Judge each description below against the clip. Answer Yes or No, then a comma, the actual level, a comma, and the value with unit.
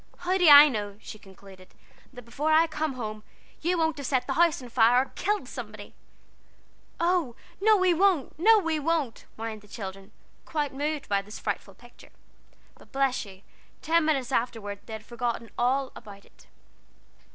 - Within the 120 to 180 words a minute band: Yes, average, 175 wpm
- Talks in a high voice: Yes, very high, 265 Hz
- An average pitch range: No, wide, 6.6 semitones